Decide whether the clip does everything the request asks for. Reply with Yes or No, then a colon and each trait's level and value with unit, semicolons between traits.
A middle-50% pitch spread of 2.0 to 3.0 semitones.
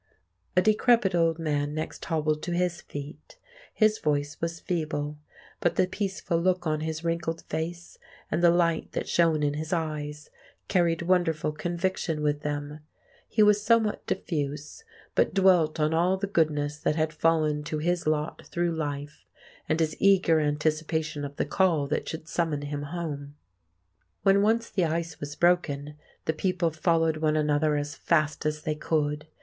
Yes: narrow, 2.5 semitones